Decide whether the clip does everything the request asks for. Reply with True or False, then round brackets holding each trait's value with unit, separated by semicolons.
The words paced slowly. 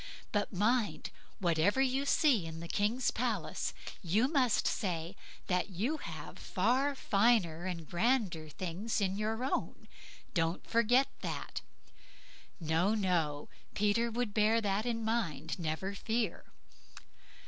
True (120 wpm)